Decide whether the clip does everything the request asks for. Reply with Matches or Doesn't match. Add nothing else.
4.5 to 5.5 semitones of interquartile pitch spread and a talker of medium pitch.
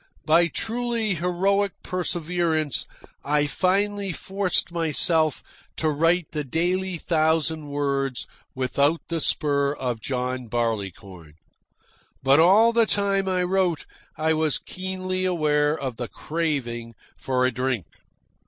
Matches